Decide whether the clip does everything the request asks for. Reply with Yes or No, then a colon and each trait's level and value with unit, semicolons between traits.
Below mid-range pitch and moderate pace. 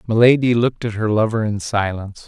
Yes: low, 110 Hz; average, 185 wpm